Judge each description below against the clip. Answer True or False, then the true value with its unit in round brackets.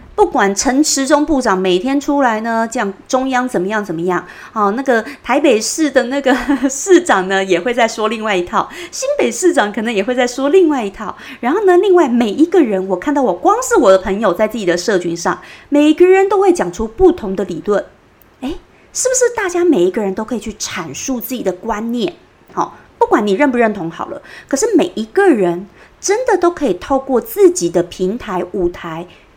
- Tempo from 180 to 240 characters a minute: False (300 characters per minute)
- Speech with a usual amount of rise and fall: False (8.5 semitones)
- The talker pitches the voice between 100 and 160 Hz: False (250 Hz)